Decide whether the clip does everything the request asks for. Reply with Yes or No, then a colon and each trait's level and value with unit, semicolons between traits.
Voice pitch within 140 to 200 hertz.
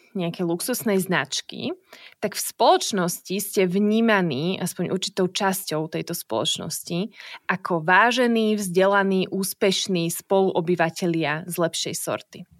Yes: medium, 185 Hz